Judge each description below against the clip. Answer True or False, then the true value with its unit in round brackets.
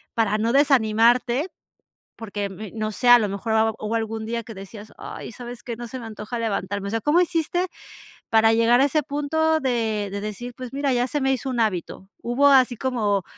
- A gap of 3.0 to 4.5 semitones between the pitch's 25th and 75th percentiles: True (3.4 semitones)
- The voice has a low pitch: False (230 Hz)